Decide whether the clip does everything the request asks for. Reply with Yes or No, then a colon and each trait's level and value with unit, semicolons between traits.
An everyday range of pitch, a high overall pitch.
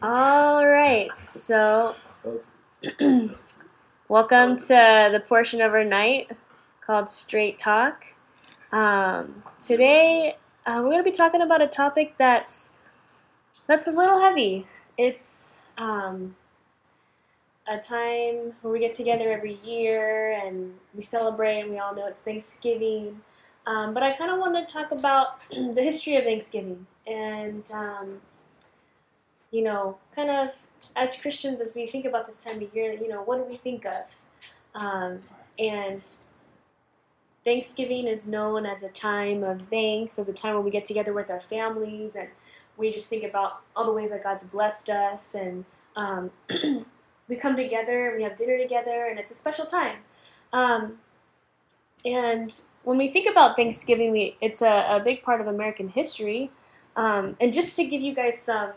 Yes: average, 3.3 semitones; high, 225 Hz